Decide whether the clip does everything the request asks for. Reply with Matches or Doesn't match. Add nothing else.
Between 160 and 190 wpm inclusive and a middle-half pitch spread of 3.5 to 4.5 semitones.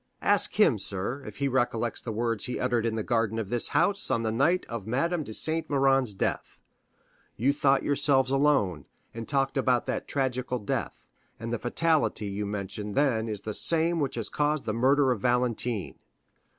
Matches